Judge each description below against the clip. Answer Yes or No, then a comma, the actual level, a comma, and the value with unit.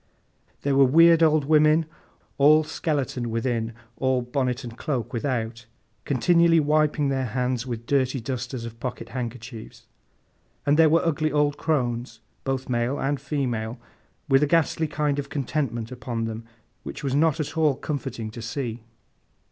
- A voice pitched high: No, low, 135 Hz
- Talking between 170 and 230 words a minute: No, average, 150 wpm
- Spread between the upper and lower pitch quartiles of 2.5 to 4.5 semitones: Yes, average, 3.9 semitones